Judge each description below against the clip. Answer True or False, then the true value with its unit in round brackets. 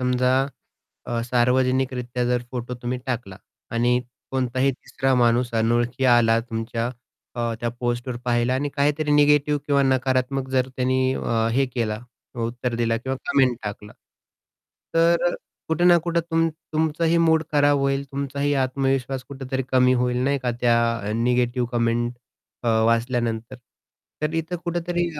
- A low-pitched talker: True (130 Hz)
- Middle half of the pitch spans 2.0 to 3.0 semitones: True (2.7 semitones)